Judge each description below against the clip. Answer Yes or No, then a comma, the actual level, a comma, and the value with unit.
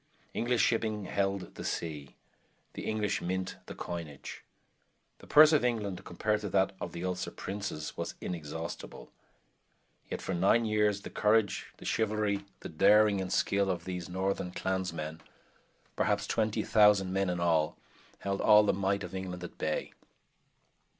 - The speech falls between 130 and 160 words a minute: Yes, average, 150 wpm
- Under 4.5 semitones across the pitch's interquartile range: Yes, average, 2.9 semitones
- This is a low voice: Yes, very low, 95 Hz